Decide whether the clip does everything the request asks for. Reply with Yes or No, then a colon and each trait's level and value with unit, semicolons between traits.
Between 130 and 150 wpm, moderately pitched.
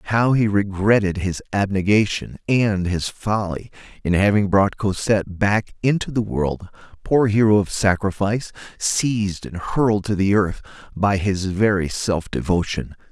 No: average, 140 wpm; low, 100 Hz